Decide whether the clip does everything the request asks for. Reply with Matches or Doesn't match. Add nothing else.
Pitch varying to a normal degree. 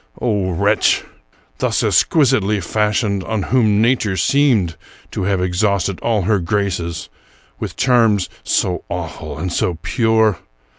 Matches